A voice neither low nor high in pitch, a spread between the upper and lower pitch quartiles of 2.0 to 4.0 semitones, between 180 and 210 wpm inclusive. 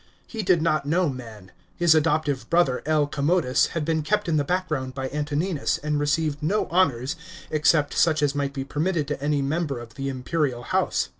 Yes: medium, 150 Hz; average, 3.1 semitones; average, 190 wpm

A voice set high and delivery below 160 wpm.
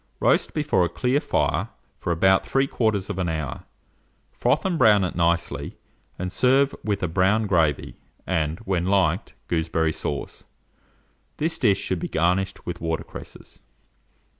No: very low, 95 Hz; average, 140 wpm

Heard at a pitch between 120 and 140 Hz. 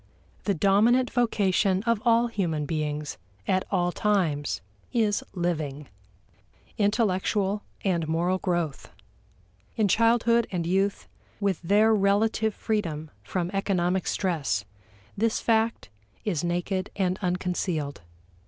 No: high, 190 Hz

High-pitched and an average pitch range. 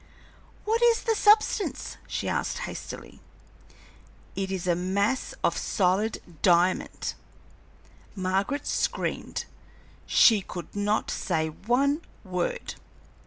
No: high, 200 Hz; wide, 7.4 semitones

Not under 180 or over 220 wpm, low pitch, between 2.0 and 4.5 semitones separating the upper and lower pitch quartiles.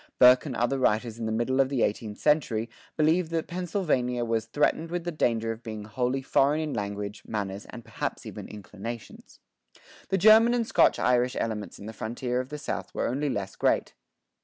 No: average, 190 wpm; low, 125 Hz; average, 5.2 semitones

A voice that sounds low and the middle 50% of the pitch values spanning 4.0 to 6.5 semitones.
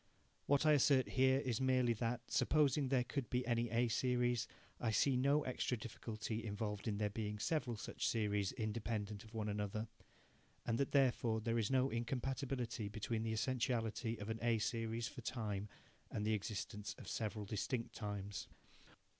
No: low, 115 Hz; average, 2.9 semitones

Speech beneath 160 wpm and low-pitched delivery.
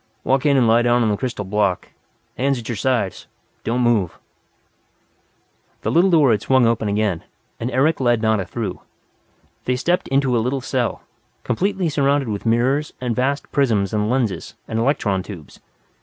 No: average, 170 wpm; low, 120 Hz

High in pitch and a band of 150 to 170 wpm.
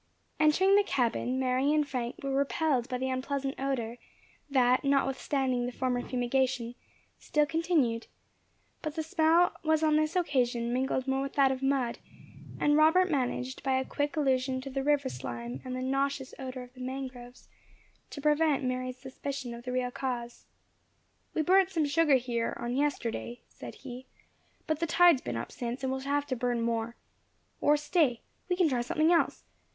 No: very high, 265 Hz; average, 180 wpm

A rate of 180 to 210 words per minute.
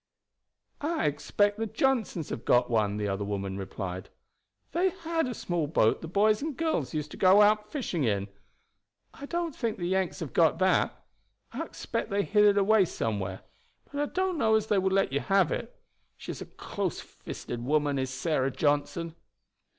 Yes: average, 185 wpm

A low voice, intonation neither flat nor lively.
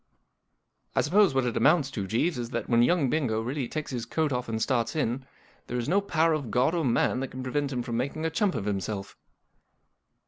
Yes: low, 130 Hz; average, 4.7 semitones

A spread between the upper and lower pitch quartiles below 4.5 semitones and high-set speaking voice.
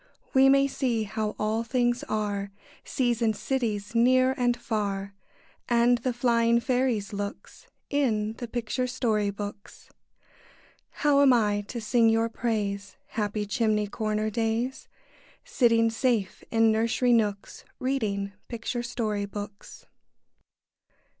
Yes: narrow, 2.6 semitones; high, 225 Hz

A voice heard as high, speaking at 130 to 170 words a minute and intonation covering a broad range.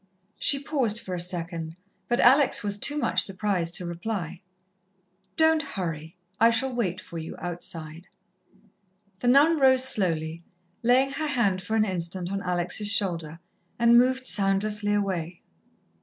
Yes: high, 200 Hz; average, 140 wpm; wide, 6.0 semitones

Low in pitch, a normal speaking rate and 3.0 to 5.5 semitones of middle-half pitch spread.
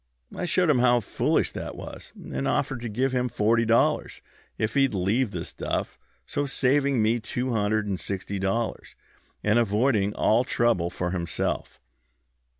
Yes: low, 115 Hz; average, 155 wpm; average, 3.6 semitones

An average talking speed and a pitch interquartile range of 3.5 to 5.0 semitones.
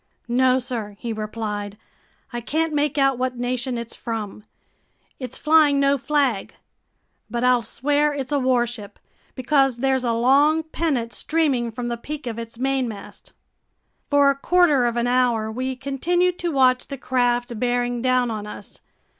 No: average, 155 wpm; average, 2.8 semitones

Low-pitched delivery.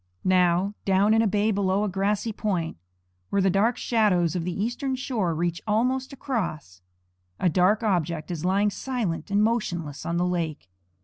No: high, 195 Hz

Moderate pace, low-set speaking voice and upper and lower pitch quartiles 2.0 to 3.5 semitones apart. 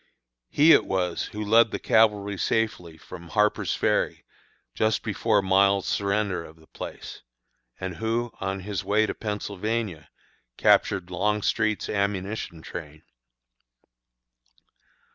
No: slow, 115 wpm; low, 100 Hz; average, 2.8 semitones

